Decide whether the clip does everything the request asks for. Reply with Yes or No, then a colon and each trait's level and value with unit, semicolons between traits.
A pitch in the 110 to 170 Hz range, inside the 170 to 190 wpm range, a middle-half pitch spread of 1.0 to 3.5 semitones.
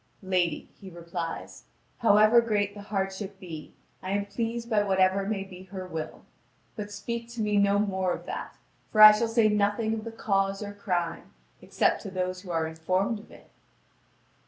No: high, 200 Hz; average, 180 wpm; narrow, 2.4 semitones